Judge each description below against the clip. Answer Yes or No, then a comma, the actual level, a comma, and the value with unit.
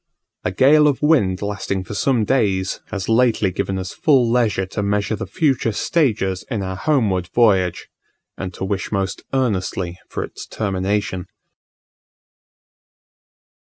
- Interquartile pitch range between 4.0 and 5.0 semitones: Yes, average, 4.5 semitones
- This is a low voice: Yes, low, 100 Hz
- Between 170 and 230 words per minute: No, slow, 135 wpm